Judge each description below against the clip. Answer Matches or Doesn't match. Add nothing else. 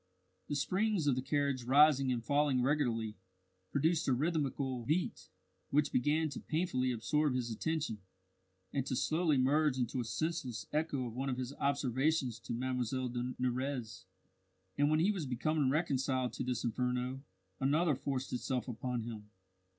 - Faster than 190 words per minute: Doesn't match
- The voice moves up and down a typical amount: Matches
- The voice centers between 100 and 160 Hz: Matches